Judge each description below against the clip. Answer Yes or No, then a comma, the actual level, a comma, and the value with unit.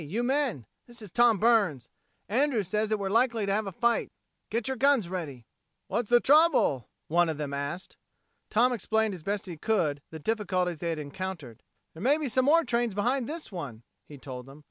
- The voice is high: Yes, high, 205 Hz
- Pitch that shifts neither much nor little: No, wide, 7.0 semitones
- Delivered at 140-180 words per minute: No, average, 200 wpm